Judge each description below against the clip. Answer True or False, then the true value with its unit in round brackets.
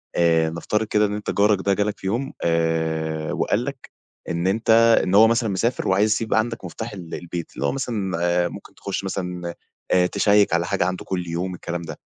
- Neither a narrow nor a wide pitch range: True (3.7 semitones)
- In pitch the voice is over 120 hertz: False (95 Hz)